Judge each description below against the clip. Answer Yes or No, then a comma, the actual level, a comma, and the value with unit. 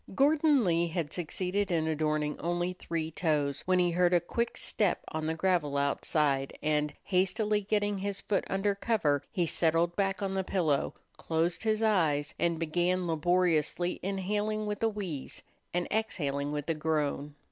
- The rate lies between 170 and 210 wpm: No, average, 160 wpm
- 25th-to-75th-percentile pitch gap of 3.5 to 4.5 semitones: Yes, average, 4.2 semitones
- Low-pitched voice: No, medium, 175 Hz